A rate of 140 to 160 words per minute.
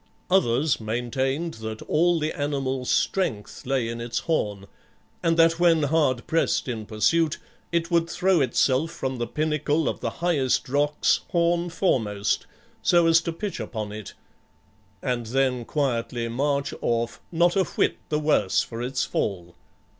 Yes: average, 150 wpm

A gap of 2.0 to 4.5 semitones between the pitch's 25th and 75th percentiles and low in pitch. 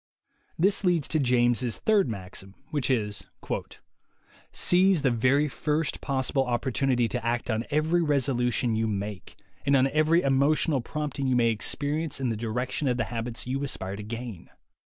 Yes: average, 4.1 semitones; low, 130 Hz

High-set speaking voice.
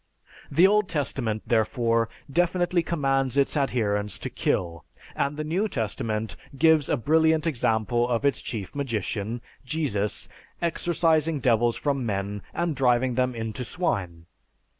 No: low, 130 Hz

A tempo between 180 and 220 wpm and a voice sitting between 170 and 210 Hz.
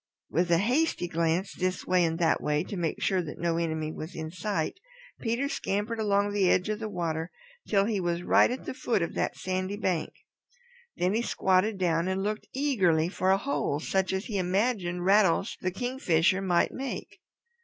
Yes: average, 190 wpm; medium, 185 Hz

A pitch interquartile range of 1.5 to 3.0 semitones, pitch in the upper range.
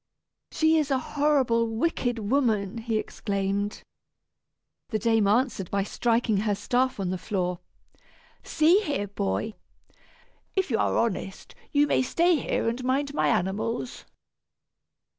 No: average, 5.1 semitones; high, 230 Hz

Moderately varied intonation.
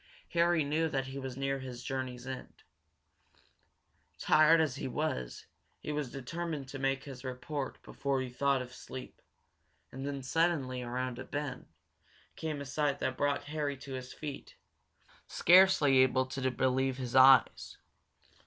No: narrow, 2.2 semitones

